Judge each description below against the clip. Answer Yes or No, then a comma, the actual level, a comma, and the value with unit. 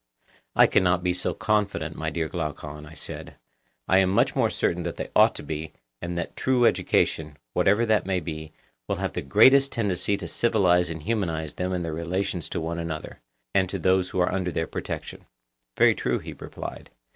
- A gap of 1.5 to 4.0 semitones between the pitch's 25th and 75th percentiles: Yes, average, 3.1 semitones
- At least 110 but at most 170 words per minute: No, average, 195 wpm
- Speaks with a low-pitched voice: Yes, very low, 90 Hz